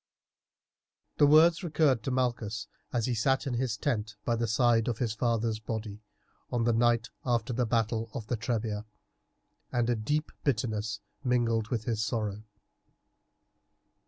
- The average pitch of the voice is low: Yes, low, 115 Hz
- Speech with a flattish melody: Yes, narrow, 2.3 semitones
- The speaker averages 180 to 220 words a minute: No, average, 150 wpm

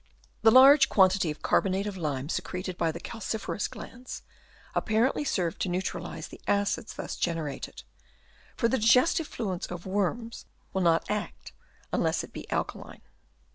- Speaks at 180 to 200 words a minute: No, average, 150 wpm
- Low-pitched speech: No, high, 195 Hz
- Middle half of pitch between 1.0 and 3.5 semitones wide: No, average, 4.5 semitones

